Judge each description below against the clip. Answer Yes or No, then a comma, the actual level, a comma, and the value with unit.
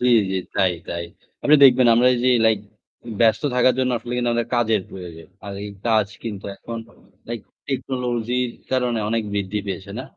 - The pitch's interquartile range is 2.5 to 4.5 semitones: Yes, average, 3.5 semitones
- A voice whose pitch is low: Yes, low, 115 Hz